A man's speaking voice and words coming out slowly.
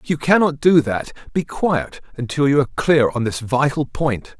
No: male; fast, 205 wpm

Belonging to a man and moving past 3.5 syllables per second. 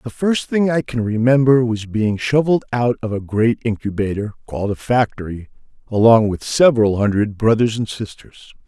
Yes: male; 5.1 syllables/s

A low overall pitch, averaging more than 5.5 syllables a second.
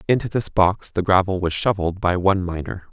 Yes: very low, 95 Hz; 6.0 syllables/s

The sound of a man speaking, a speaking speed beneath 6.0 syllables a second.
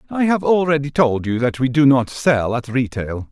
Yes: male; 4.8 syllables/s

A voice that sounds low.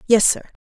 No: high, 220 Hz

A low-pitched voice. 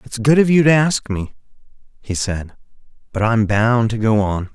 Yes: low, 115 Hz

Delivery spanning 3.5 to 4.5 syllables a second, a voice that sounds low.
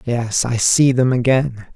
Yes: 3.8 syllables/s; low, 125 Hz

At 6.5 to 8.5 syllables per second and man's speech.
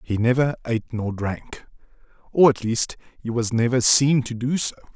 No: 5.1 syllables/s; male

